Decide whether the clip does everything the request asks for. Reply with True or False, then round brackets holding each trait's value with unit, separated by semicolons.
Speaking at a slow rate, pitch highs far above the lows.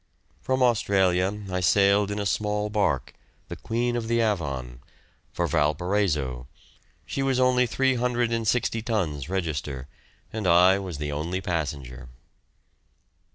True (120 wpm; 6.9 semitones)